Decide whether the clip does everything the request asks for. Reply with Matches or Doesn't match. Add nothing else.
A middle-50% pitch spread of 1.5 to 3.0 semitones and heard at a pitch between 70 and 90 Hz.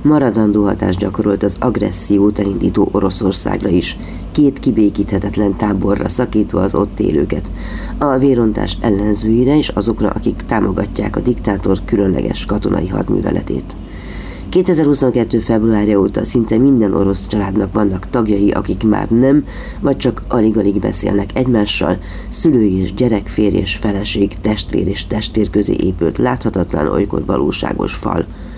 Doesn't match